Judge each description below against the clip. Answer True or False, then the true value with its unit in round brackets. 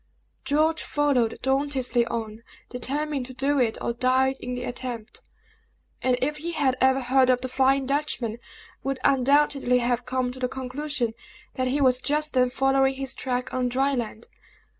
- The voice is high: True (260 Hz)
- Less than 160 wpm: False (165 wpm)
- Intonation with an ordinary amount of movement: False (1.8 semitones)